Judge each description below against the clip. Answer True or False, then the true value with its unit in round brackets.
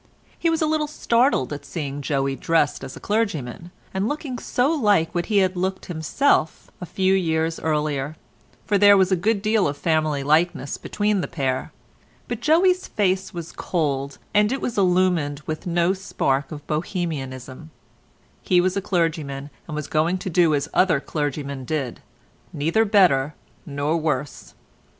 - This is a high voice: False (165 Hz)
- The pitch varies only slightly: False (5.1 semitones)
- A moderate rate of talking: True (160 wpm)